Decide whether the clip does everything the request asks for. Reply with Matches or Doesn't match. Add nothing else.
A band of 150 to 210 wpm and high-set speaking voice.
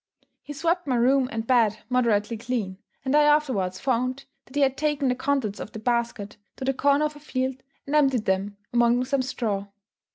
Matches